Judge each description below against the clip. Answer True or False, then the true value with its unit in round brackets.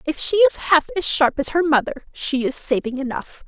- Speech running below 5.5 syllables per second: True (5.2 syllables/s)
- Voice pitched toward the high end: True (280 Hz)